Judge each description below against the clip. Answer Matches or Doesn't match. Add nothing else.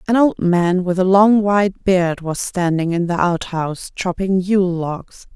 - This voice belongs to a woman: Matches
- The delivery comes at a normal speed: Matches